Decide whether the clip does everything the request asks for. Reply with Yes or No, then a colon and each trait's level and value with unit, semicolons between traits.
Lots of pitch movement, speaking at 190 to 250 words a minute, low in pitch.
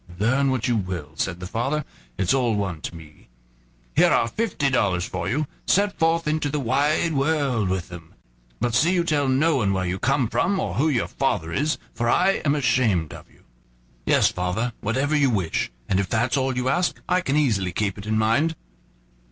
Yes: wide, 7.5 semitones; average, 200 wpm; low, 125 Hz